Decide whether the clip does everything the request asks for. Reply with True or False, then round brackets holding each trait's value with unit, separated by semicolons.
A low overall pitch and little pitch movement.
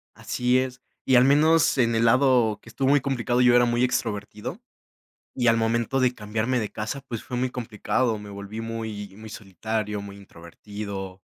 False (115 Hz; 3.1 semitones)